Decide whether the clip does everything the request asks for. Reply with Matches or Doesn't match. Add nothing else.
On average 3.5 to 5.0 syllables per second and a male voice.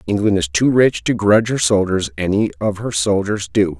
Doesn't match